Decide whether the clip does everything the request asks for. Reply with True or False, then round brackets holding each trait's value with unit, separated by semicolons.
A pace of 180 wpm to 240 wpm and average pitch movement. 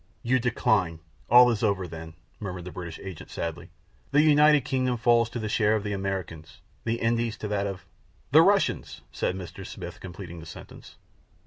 True (185 wpm; 4.8 semitones)